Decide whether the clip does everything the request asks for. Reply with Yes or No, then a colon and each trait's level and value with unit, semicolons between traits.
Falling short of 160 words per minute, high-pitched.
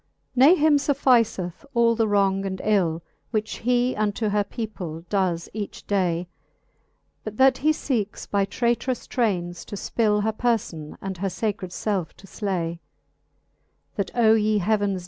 Yes: average, 150 wpm; high, 210 Hz